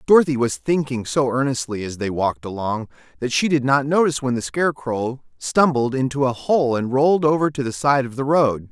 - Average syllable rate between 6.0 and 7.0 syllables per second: No, 5.5 syllables/s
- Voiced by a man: Yes, male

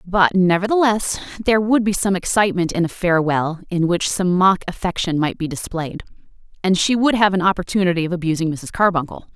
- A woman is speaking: Yes, female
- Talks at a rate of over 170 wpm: Yes, average, 180 wpm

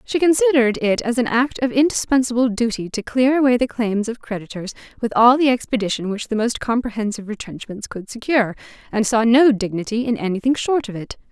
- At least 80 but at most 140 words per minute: No, average, 190 wpm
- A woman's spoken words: Yes, female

